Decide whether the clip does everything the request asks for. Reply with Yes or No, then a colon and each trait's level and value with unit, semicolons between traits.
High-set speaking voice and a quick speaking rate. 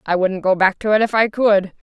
Yes: high, 200 Hz; fast, 280 wpm